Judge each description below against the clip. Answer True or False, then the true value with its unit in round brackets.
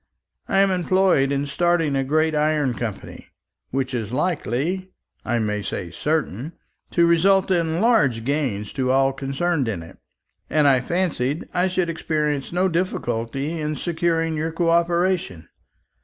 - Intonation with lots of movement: False (4.6 semitones)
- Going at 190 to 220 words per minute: False (145 wpm)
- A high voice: False (155 Hz)